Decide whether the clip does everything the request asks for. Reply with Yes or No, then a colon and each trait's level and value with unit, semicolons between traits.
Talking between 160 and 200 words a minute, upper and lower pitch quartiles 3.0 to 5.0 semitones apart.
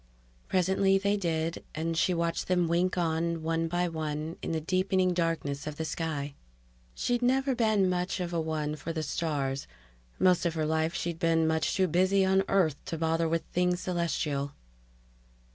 No: average, 175 wpm; narrow, 2.4 semitones